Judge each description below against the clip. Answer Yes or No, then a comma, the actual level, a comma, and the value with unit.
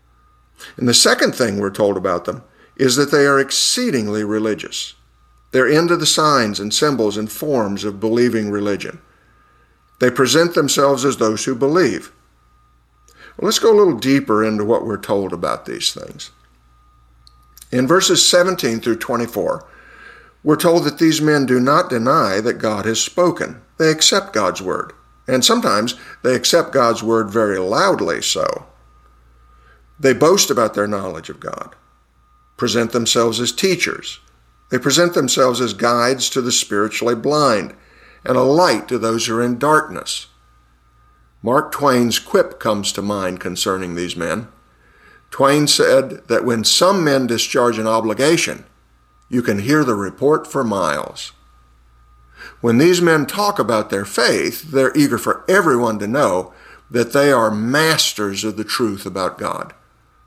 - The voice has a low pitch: Yes, low, 110 Hz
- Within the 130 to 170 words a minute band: Yes, average, 150 wpm